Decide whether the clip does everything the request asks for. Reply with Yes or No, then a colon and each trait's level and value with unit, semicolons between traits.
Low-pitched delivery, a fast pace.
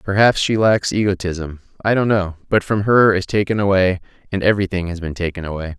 No: very low, 95 Hz; average, 195 wpm